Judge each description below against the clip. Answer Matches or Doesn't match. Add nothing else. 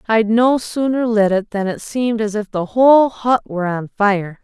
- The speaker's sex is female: Matches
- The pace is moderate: Doesn't match